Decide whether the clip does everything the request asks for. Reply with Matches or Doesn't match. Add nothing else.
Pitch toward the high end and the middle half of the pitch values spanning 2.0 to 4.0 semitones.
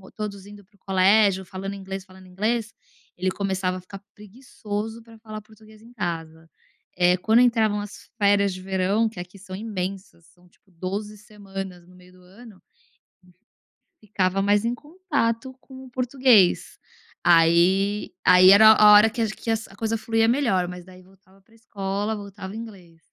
Matches